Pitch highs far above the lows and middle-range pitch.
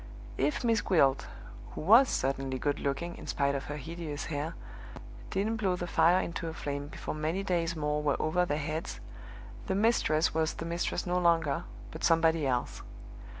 No: average, 3.3 semitones; medium, 160 Hz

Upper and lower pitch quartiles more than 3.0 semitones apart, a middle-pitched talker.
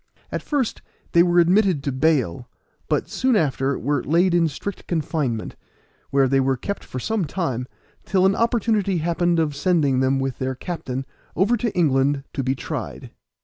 Yes: wide, 5.6 semitones; medium, 160 Hz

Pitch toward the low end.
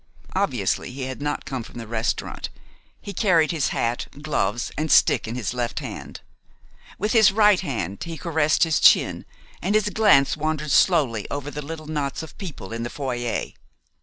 No: medium, 145 Hz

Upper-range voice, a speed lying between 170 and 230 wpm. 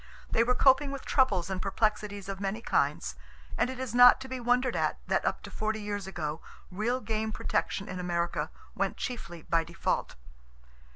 Yes: high, 215 Hz; average, 180 wpm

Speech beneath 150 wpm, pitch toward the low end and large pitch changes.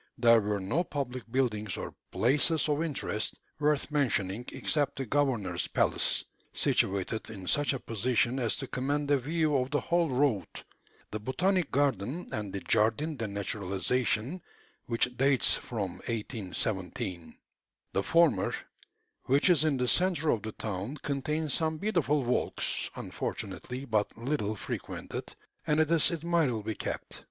Yes: average, 140 wpm; low, 130 Hz; wide, 5.7 semitones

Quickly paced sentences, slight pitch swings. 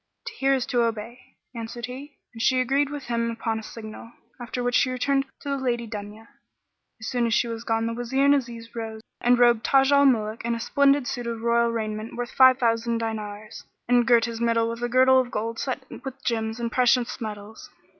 Yes: fast, 215 wpm; narrow, 2.1 semitones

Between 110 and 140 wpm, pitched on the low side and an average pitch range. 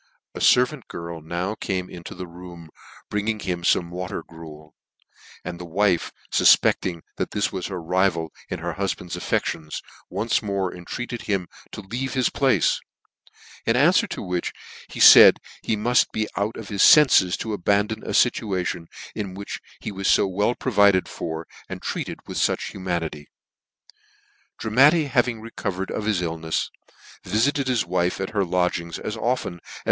No: average, 160 wpm; very low, 95 Hz; average, 4.1 semitones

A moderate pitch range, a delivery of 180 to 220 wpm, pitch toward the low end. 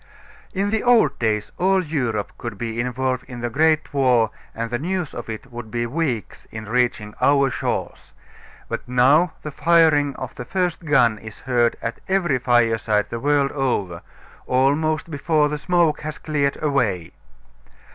No: average, 4.8 semitones; average, 160 wpm; low, 130 Hz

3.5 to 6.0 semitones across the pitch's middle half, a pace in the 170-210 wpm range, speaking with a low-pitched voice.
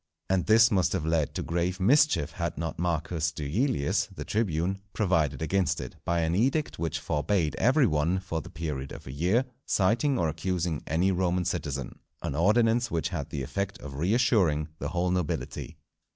Yes: average, 3.9 semitones; average, 175 wpm; very low, 85 Hz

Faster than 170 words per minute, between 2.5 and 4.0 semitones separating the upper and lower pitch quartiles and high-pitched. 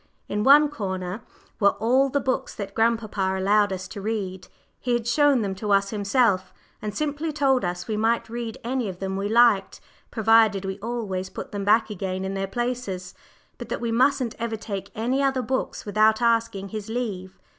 Yes: average, 190 wpm; average, 3.6 semitones; high, 220 Hz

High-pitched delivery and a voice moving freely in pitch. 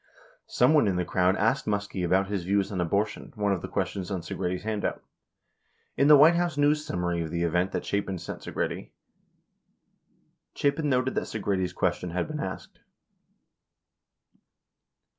No: low, 100 Hz; wide, 6.0 semitones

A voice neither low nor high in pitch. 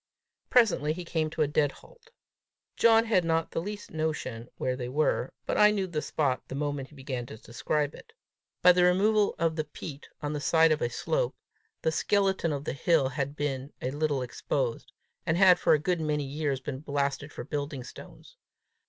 Yes: medium, 150 Hz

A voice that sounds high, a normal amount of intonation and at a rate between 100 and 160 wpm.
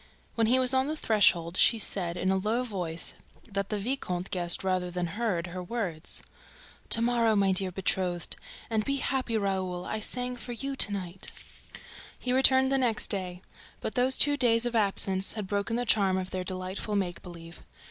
No: high, 200 Hz; average, 4.6 semitones; average, 190 wpm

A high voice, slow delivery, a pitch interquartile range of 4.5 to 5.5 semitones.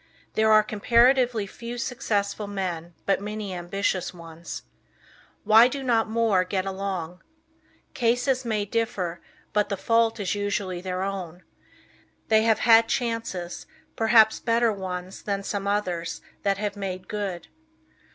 No: high, 205 Hz; slow, 130 wpm; average, 3.4 semitones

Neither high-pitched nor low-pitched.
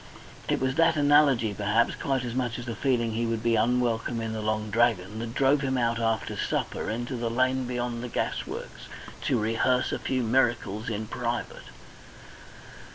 No: low, 120 Hz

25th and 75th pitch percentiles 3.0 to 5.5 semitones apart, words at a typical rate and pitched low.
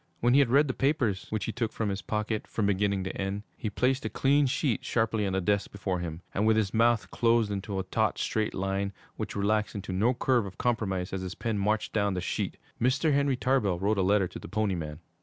No: average, 3.4 semitones; fast, 240 wpm; low, 105 Hz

